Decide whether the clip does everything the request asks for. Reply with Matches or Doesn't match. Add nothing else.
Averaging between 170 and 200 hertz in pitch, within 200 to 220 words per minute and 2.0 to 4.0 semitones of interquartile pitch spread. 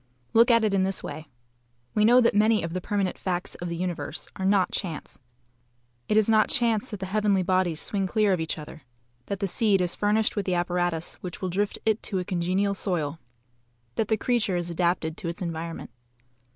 Matches